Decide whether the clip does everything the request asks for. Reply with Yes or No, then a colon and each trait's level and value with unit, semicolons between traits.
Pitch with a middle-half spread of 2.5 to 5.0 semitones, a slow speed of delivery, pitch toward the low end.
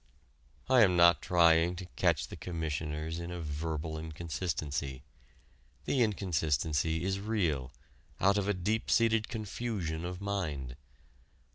Yes: average, 4.2 semitones; slow, 125 wpm; very low, 85 Hz